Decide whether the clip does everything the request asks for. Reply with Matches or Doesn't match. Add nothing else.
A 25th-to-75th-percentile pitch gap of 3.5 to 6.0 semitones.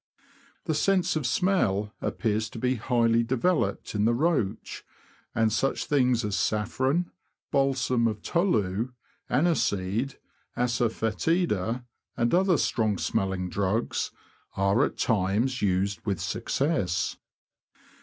Matches